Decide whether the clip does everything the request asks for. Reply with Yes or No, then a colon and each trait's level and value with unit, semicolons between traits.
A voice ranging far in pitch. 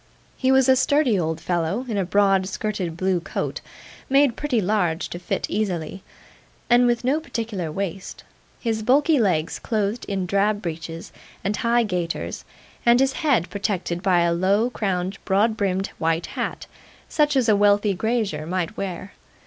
No: average, 4.7 semitones